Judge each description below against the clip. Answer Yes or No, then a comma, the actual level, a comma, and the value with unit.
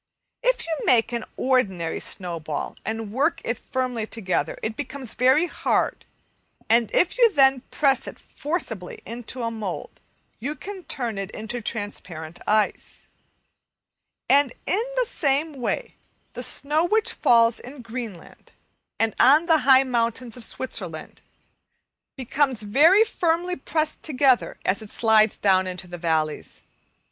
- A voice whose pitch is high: Yes, high, 245 Hz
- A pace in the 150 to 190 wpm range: No, slow, 135 wpm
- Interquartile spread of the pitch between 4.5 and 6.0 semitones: Yes, average, 5.2 semitones